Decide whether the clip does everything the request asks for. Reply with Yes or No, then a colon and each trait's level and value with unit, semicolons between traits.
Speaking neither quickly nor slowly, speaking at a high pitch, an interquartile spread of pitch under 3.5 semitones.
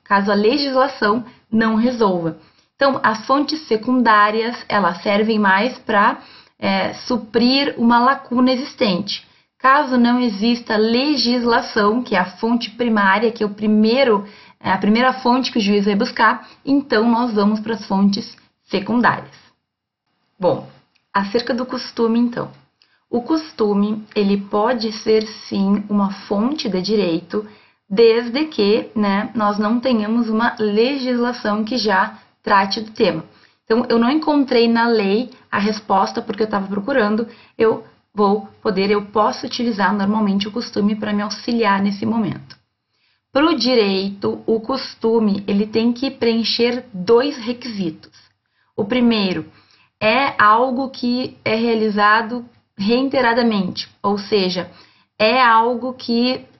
Yes: average, 135 wpm; high, 225 Hz; average, 2.8 semitones